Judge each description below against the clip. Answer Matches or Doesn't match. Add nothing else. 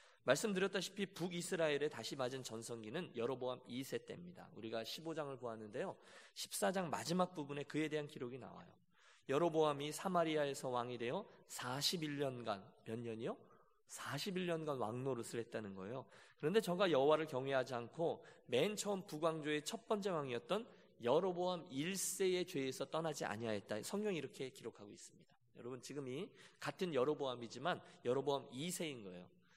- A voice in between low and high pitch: Matches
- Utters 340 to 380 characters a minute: Matches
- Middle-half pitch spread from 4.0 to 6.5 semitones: Matches